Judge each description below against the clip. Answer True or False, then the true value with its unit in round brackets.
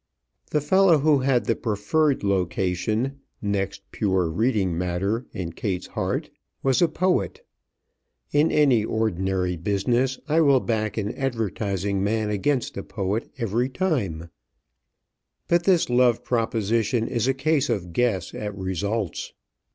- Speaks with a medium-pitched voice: False (110 Hz)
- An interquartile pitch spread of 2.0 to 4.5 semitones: False (5.5 semitones)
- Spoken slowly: True (130 wpm)